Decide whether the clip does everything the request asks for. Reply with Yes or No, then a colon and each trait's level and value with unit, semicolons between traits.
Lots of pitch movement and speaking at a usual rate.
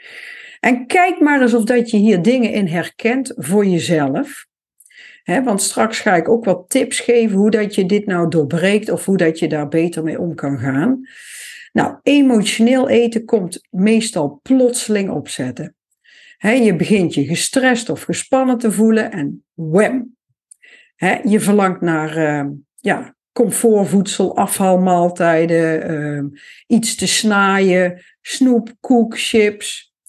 No: wide, 6.1 semitones; slow, 130 wpm